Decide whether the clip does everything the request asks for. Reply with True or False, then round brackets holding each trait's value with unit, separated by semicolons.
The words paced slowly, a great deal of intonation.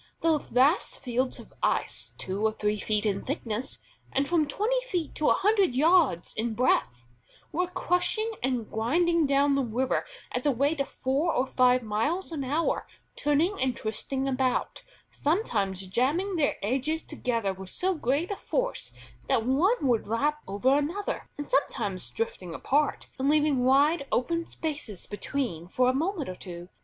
False (165 wpm; 6.0 semitones)